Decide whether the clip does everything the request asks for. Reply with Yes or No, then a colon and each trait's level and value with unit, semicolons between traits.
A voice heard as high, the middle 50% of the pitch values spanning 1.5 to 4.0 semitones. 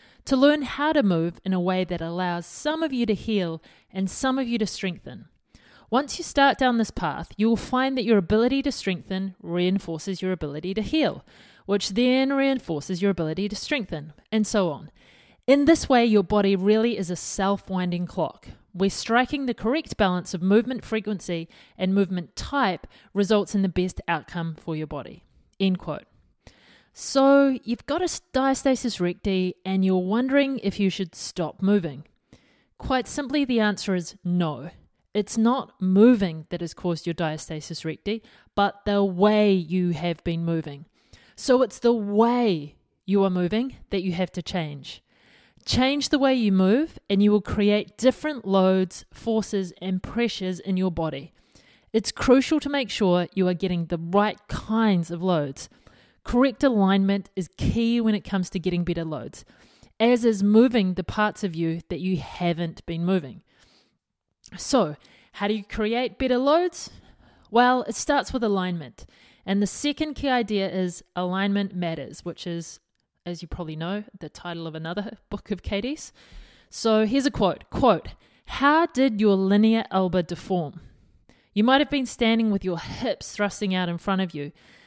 No: high, 200 Hz; average, 4.9 semitones